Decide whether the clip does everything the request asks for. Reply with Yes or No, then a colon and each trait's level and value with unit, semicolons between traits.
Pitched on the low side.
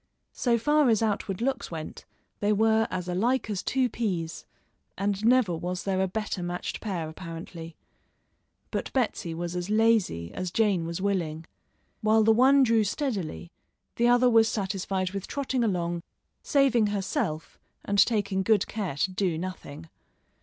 No: high, 200 Hz